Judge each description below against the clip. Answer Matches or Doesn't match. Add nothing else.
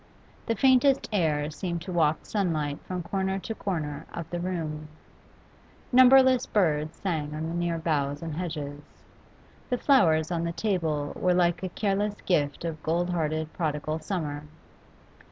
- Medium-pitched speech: Matches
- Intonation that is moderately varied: Matches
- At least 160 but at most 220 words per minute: Doesn't match